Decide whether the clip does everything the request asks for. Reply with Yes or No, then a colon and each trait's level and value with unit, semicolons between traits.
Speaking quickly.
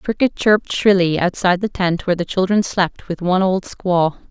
Yes: fast, 210 wpm